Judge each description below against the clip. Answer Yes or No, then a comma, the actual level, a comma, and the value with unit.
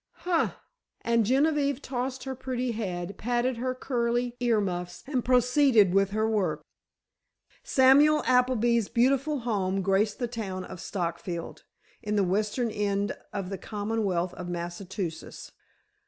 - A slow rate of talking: Yes, slow, 130 wpm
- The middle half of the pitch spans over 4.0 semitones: Yes, average, 4.7 semitones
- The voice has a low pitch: No, high, 225 Hz